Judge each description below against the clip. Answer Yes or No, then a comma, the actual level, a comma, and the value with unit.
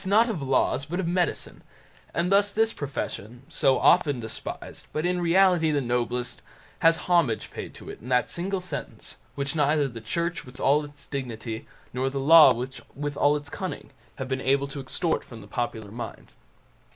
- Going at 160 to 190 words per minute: Yes, average, 180 wpm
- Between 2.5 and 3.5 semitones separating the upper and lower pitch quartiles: No, average, 5.2 semitones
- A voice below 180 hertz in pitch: Yes, medium, 140 Hz